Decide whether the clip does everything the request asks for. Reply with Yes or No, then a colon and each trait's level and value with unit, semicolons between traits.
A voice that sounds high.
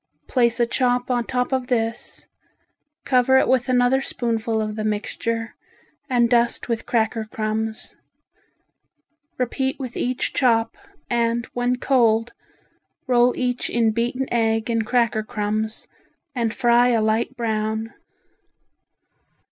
Yes: high, 235 Hz